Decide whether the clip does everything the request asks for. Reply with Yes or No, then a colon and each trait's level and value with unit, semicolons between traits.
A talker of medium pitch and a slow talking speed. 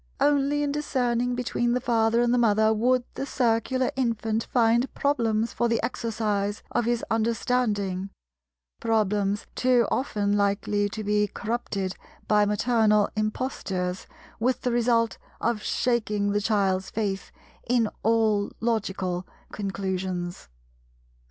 No: high, 220 Hz; slow, 120 wpm